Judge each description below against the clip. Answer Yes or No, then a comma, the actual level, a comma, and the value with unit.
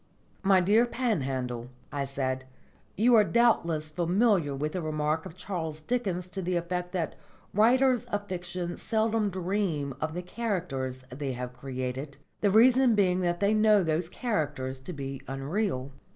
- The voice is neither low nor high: Yes, medium, 175 Hz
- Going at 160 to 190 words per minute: No, average, 150 wpm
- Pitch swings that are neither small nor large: No, wide, 6.7 semitones